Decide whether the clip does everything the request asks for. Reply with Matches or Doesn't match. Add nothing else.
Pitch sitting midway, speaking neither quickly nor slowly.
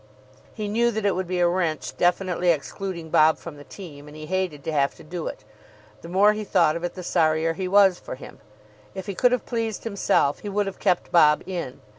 Doesn't match